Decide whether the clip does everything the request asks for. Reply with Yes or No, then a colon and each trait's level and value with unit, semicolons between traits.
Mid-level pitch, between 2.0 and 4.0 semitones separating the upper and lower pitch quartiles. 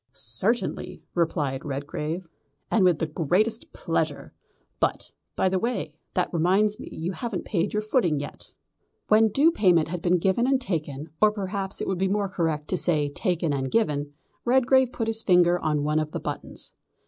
No: medium, 180 Hz; wide, 5.5 semitones